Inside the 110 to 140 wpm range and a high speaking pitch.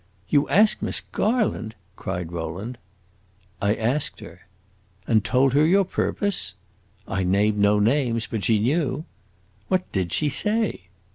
No: slow, 135 wpm; low, 120 Hz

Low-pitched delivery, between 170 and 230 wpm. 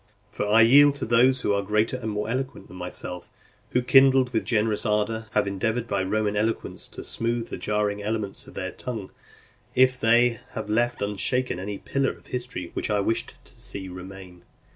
Yes: low, 110 Hz; average, 185 wpm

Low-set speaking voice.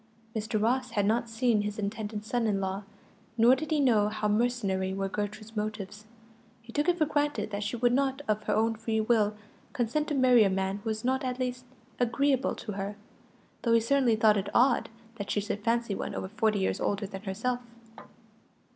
No: high, 220 Hz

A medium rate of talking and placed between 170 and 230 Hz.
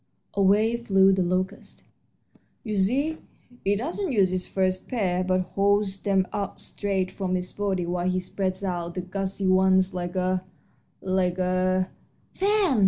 Yes: average, 155 wpm; high, 190 Hz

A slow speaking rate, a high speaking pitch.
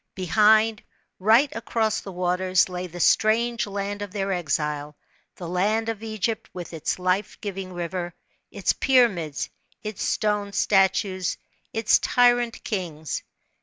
Yes: slow, 130 wpm; high, 195 Hz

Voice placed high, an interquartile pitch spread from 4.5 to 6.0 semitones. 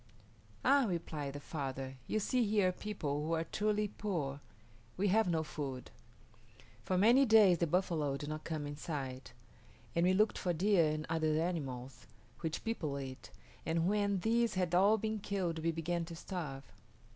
No: medium, 170 Hz; average, 5.3 semitones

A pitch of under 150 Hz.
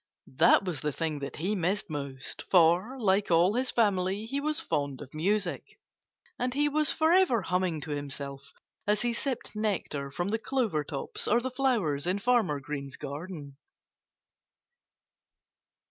No: medium, 185 Hz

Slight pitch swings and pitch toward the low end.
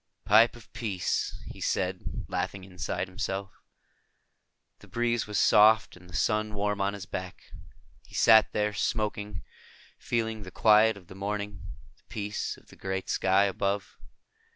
Yes: narrow, 2.0 semitones; low, 105 Hz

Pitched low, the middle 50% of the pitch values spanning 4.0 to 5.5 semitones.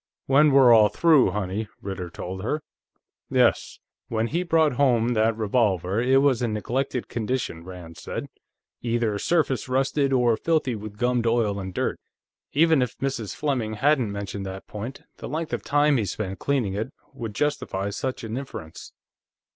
Yes: low, 120 Hz; average, 4.8 semitones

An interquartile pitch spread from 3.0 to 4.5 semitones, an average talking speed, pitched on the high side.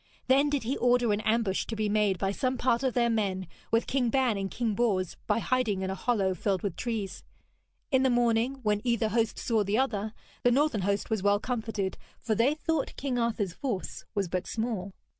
No: average, 3.6 semitones; fast, 210 wpm; high, 225 Hz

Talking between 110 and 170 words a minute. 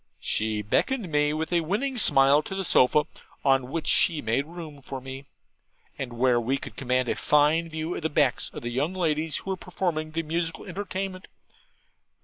No: average, 185 wpm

